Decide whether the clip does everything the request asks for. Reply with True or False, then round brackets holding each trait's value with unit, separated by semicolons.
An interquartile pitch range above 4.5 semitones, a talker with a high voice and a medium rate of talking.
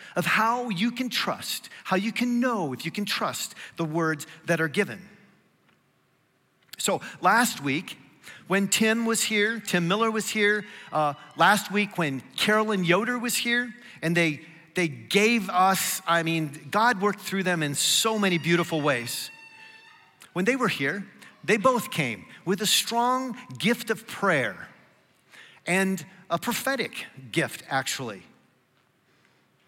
True (5.1 semitones; 200 Hz; 145 wpm)